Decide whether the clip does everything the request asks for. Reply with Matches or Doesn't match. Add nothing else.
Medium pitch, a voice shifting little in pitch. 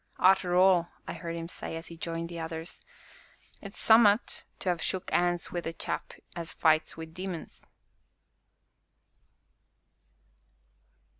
Matches